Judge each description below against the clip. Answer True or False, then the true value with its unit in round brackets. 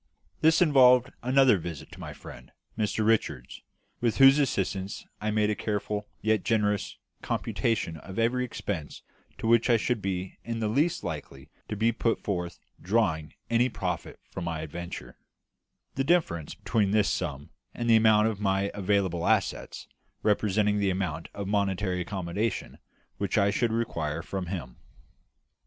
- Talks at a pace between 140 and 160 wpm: True (150 wpm)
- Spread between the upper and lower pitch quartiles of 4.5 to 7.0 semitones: False (4.1 semitones)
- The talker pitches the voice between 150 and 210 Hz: False (105 Hz)